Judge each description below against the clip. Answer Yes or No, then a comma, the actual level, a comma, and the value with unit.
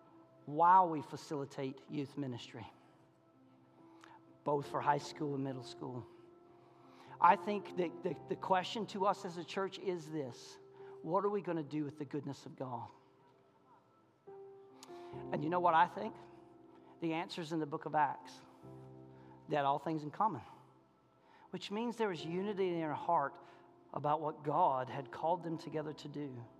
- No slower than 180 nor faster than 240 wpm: No, average, 160 wpm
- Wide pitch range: Yes, wide, 5.9 semitones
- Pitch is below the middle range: No, medium, 150 Hz